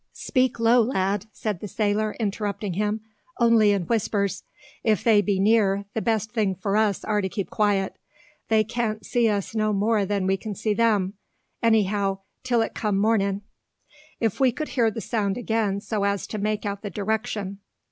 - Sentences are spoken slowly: No, average, 175 wpm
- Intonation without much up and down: Yes, narrow, 2.0 semitones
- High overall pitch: Yes, high, 210 Hz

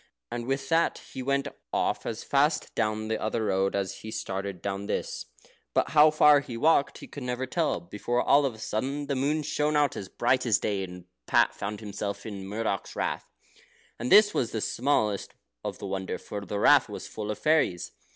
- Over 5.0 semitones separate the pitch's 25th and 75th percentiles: Yes, wide, 5.6 semitones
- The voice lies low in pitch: Yes, low, 115 Hz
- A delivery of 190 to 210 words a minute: Yes, fast, 205 wpm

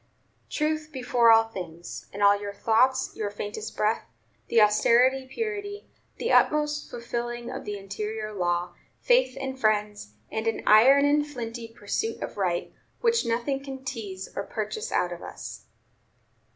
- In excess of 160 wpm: No, average, 150 wpm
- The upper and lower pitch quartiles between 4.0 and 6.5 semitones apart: Yes, average, 4.6 semitones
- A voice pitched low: No, high, 230 Hz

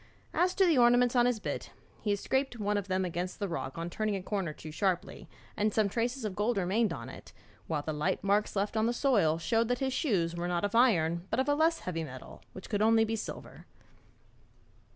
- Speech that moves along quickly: Yes, fast, 230 wpm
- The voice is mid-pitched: No, high, 205 Hz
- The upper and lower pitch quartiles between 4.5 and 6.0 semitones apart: Yes, average, 5.3 semitones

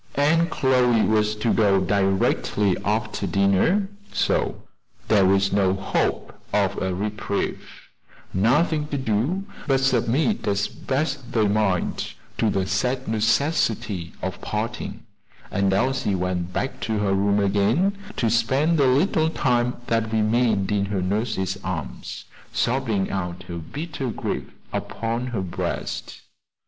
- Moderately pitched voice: No, low, 110 Hz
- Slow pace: Yes, slow, 130 wpm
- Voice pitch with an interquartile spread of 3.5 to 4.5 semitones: No, average, 5.0 semitones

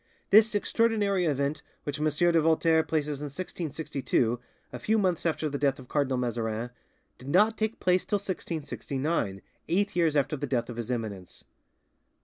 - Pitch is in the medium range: Yes, medium, 150 Hz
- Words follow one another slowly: No, average, 160 wpm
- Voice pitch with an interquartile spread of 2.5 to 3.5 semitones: No, wide, 5.4 semitones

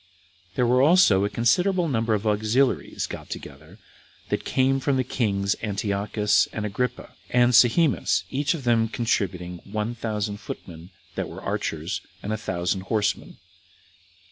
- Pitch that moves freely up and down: No, average, 3.9 semitones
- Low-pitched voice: Yes, low, 110 Hz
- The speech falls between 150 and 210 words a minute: No, average, 140 wpm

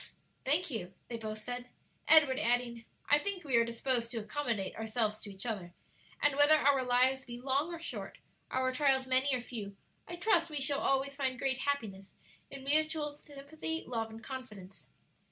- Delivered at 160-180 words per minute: Yes, average, 175 wpm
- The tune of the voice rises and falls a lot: No, average, 3.8 semitones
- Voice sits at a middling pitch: No, very high, 260 Hz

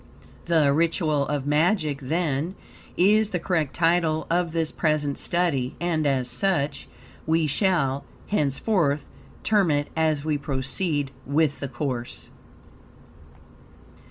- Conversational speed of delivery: No, slow, 115 wpm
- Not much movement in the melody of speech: No, average, 3.4 semitones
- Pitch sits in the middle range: Yes, medium, 155 Hz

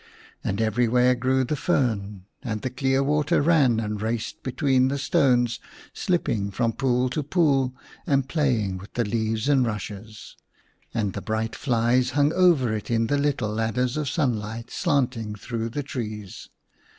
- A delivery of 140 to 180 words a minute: Yes, average, 160 wpm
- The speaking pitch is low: Yes, low, 125 Hz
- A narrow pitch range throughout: No, average, 3.7 semitones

